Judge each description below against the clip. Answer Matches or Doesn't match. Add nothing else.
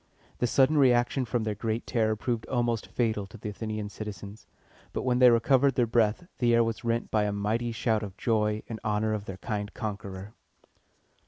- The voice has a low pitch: Matches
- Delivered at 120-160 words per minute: Doesn't match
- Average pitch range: Doesn't match